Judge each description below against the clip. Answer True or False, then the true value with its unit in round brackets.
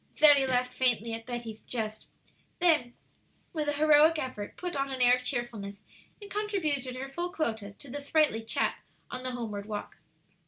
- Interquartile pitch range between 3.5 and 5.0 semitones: True (4.7 semitones)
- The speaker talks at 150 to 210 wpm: True (170 wpm)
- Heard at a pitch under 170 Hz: False (255 Hz)